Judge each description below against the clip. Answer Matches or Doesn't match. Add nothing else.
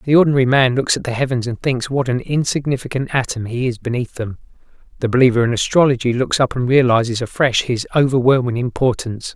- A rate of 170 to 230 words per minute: Matches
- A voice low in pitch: Matches